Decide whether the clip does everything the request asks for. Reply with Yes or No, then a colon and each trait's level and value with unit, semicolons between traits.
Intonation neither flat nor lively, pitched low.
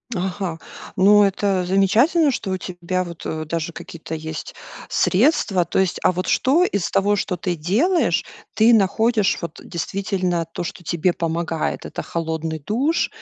No: average, 3.5 semitones; medium, 185 Hz